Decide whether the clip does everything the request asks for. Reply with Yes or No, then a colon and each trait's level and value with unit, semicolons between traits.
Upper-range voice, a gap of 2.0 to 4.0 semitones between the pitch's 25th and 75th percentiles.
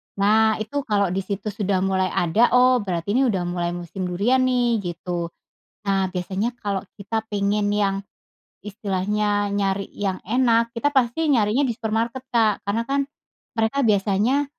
Yes: high, 205 Hz; average, 3.2 semitones